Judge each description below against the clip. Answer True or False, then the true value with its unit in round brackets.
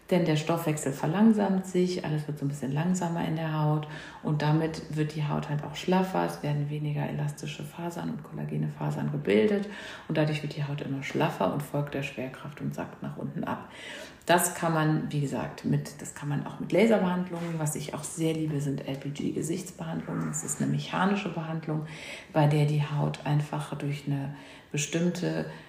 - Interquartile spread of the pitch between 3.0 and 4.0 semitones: False (2.6 semitones)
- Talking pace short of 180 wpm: False (185 wpm)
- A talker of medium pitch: True (150 Hz)